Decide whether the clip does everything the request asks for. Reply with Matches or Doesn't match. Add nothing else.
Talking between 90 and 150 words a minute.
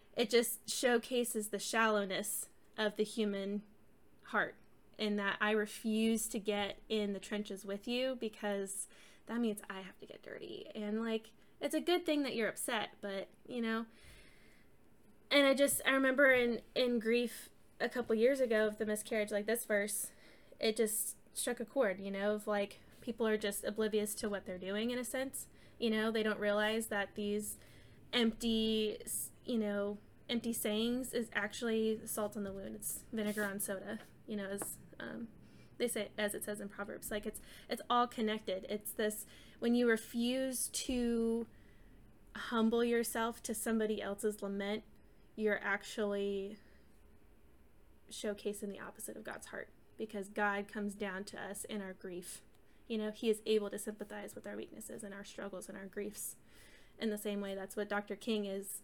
Doesn't match